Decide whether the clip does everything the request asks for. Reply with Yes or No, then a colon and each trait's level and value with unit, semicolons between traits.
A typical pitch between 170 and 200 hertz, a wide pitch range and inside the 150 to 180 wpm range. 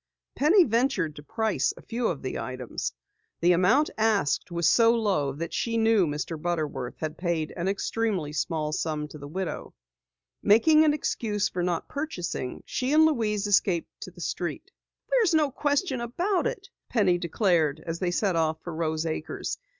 Yes: medium, 185 Hz; wide, 6.5 semitones; average, 170 wpm